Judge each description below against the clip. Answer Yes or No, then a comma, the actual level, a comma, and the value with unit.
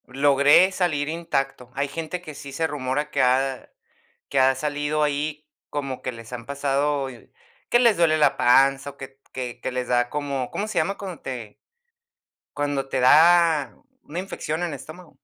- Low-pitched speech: No, medium, 145 Hz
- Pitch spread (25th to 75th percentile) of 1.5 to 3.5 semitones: Yes, average, 2.8 semitones